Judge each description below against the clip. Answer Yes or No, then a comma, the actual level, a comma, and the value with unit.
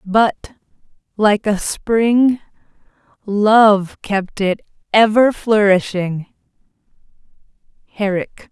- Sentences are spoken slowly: Yes, slow, 70 wpm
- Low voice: No, high, 210 Hz